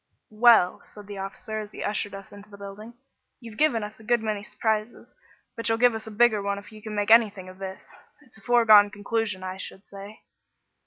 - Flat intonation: Yes, narrow, 1.9 semitones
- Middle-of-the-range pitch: No, high, 210 Hz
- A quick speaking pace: Yes, fast, 215 wpm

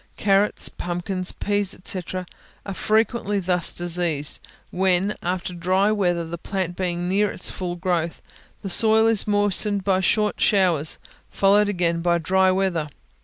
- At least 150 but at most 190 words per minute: No, average, 140 wpm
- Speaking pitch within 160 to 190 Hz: Yes, medium, 185 Hz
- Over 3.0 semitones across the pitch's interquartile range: No, narrow, 2.6 semitones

